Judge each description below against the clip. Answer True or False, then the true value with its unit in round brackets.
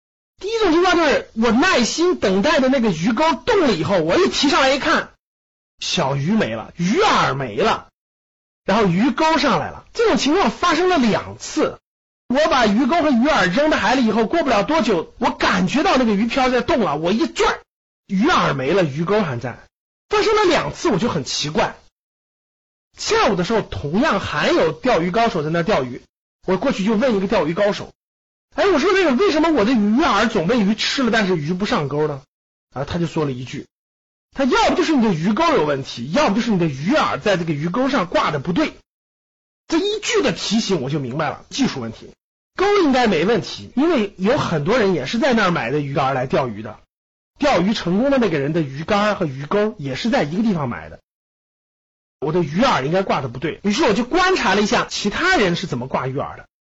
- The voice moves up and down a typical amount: False (8.3 semitones)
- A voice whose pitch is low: False (225 Hz)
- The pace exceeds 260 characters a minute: True (300 characters per minute)